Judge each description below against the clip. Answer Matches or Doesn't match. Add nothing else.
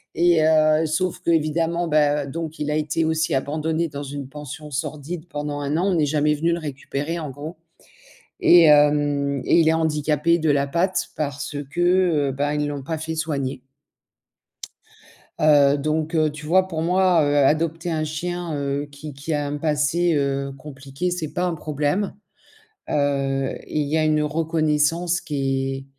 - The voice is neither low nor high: Matches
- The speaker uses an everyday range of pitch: Doesn't match